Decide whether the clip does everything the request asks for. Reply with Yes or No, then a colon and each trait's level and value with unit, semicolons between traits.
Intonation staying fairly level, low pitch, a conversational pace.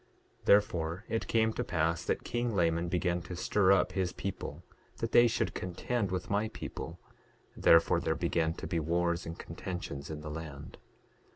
No: average, 3.3 semitones; very low, 90 Hz; average, 175 wpm